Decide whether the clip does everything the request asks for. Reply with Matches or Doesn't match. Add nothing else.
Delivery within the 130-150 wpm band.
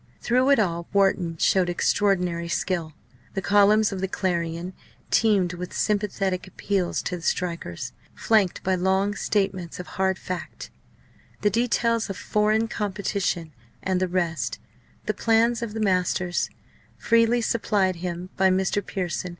Matches